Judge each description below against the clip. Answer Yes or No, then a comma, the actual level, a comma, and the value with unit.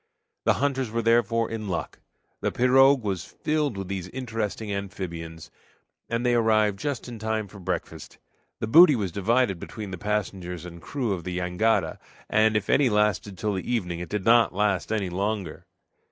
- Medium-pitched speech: No, low, 105 Hz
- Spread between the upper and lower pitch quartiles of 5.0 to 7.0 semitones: No, average, 3.7 semitones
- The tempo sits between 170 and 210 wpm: Yes, average, 175 wpm